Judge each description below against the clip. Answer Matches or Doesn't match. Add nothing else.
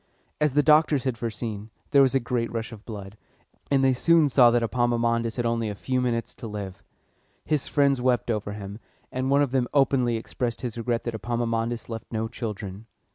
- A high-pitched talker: Doesn't match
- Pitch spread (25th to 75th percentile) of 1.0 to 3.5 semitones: Matches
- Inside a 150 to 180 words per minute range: Doesn't match